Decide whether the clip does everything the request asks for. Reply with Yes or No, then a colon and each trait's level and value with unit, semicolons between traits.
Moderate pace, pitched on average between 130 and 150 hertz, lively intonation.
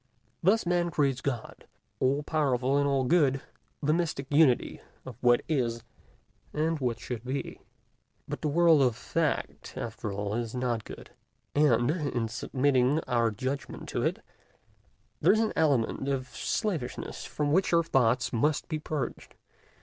No: average, 150 wpm; low, 135 Hz; average, 4.0 semitones